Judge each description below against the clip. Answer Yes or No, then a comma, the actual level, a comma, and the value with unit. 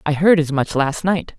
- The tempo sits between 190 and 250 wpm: No, fast, 260 wpm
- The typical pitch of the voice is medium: Yes, medium, 160 Hz